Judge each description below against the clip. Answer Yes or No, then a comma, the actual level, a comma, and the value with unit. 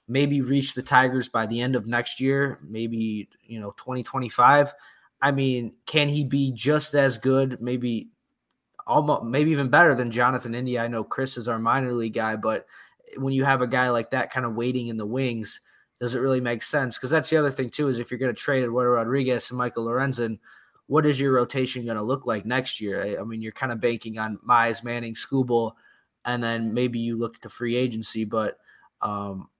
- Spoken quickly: Yes, fast, 215 wpm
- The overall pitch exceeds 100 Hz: Yes, low, 125 Hz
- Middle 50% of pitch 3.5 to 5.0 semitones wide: No, narrow, 2.4 semitones